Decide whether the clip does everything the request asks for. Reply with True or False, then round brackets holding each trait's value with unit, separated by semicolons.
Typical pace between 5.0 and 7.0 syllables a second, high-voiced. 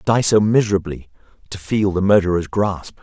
False (5.4 syllables/s; 95 Hz)